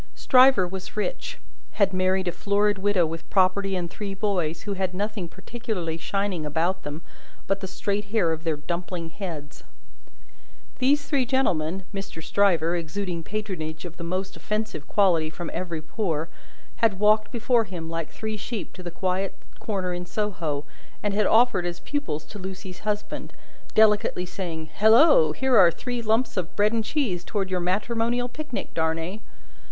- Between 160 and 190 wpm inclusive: Yes, average, 165 wpm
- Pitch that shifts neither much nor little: Yes, average, 3.8 semitones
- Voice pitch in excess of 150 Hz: Yes, high, 190 Hz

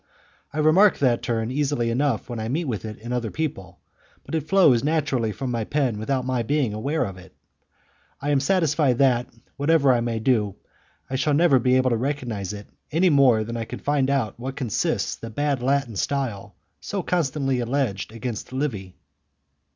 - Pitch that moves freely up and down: No, average, 4.0 semitones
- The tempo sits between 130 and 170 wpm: No, average, 190 wpm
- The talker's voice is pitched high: No, low, 130 Hz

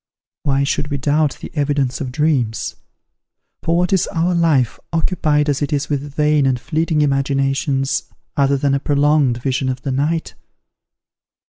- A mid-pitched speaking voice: Yes, medium, 145 Hz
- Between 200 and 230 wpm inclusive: No, average, 155 wpm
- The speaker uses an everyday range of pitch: No, narrow, 2.0 semitones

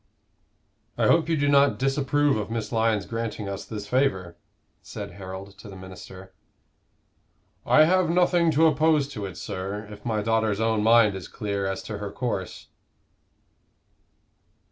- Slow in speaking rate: No, average, 150 wpm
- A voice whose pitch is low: Yes, low, 110 Hz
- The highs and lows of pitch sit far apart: Yes, wide, 5.9 semitones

